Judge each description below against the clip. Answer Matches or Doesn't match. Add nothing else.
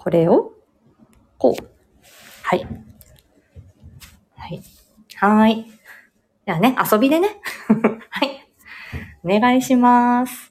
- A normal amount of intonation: Matches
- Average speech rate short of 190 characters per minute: Matches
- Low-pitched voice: Doesn't match